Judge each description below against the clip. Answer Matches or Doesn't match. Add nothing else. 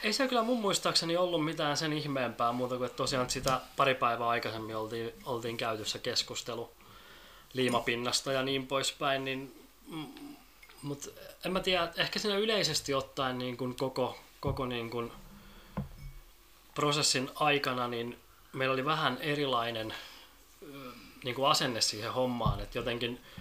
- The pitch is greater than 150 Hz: Doesn't match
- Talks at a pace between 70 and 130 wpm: Doesn't match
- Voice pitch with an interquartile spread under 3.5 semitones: Doesn't match